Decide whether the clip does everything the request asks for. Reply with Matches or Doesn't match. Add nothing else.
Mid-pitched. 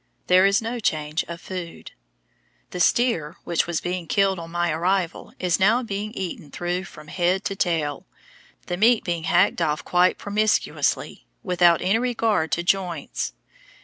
Matches